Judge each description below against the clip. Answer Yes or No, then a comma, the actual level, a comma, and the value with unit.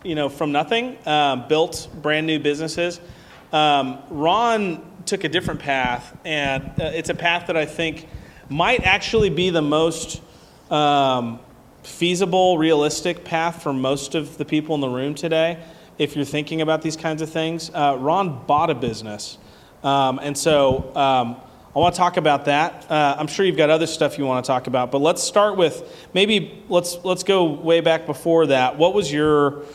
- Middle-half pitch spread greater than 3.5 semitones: No, average, 3.2 semitones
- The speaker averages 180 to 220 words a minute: Yes, average, 185 wpm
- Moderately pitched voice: Yes, medium, 155 Hz